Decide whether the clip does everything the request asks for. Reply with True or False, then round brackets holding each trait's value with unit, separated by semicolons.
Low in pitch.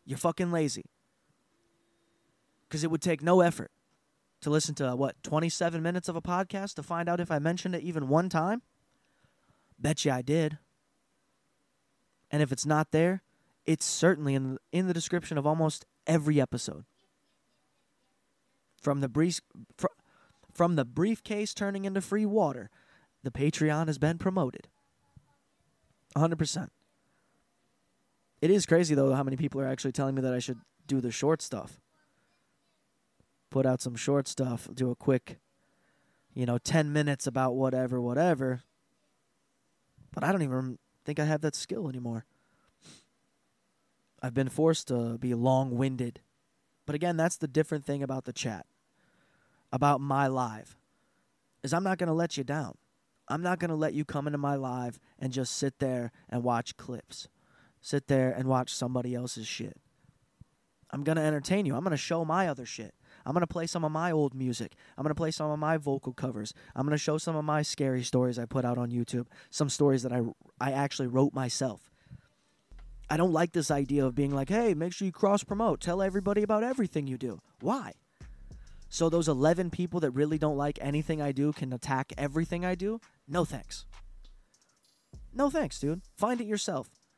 False (150 Hz)